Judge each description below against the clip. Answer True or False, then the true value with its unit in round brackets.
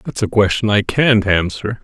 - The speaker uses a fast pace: False (195 wpm)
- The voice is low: True (105 Hz)